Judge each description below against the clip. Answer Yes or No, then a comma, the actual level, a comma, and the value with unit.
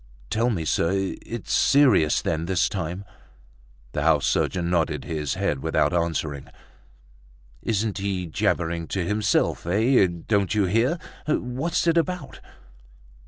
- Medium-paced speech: No, slow, 125 wpm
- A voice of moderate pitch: No, very low, 95 Hz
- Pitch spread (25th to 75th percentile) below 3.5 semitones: No, wide, 5.5 semitones